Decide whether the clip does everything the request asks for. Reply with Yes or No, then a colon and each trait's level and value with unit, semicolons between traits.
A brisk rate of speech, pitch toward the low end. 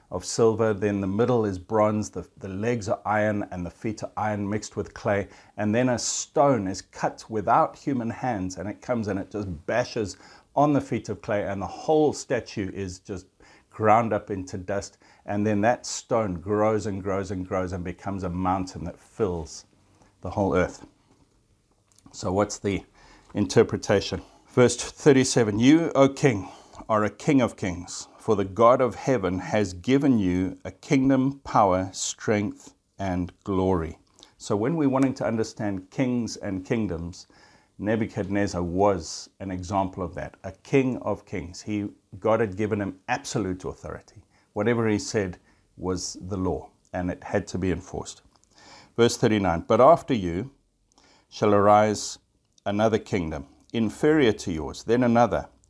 No: average, 160 wpm; low, 105 Hz